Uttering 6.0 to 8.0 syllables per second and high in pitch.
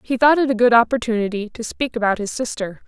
Yes: 6.2 syllables/s; high, 230 Hz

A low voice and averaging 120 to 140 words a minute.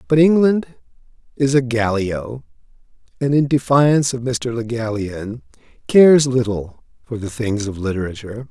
Yes: low, 120 Hz; slow, 135 wpm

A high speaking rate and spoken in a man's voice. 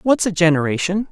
No: average, 160 wpm; male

